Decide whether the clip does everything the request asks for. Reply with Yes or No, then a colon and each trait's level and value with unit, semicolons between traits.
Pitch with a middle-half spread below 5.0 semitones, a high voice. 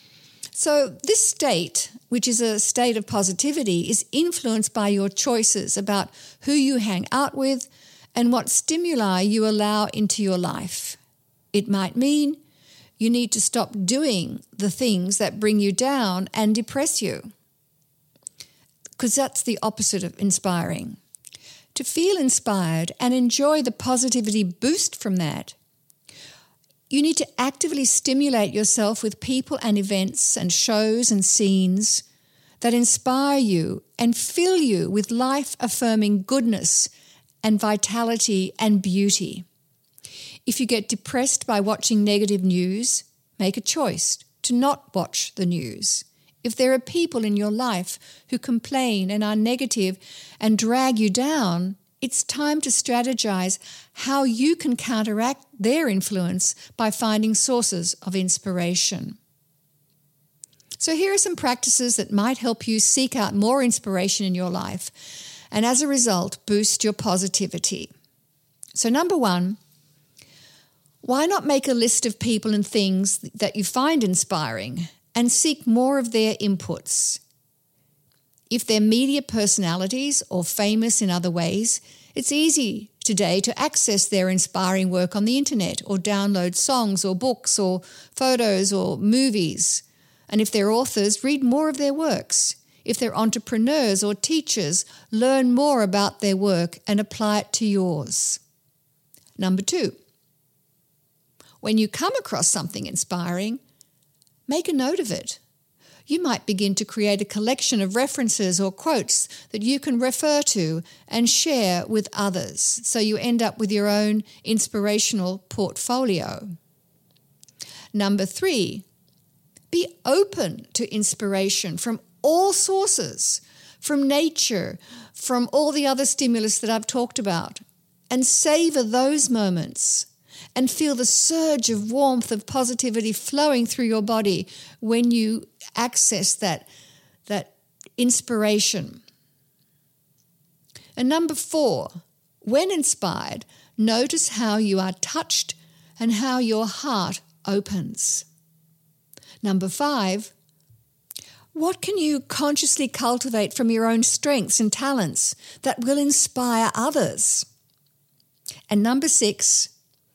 No: average, 5.3 semitones; high, 215 Hz